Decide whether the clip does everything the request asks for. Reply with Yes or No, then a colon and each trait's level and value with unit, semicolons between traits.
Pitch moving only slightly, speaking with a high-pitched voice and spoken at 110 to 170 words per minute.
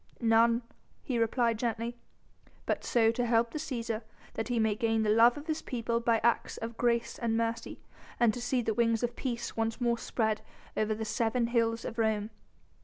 No: narrow, 1.1 semitones; high, 230 Hz; average, 190 wpm